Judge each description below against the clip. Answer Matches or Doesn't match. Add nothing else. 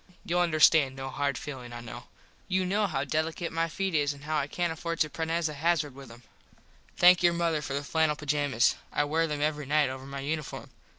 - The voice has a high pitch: Doesn't match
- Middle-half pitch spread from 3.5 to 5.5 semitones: Doesn't match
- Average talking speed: Doesn't match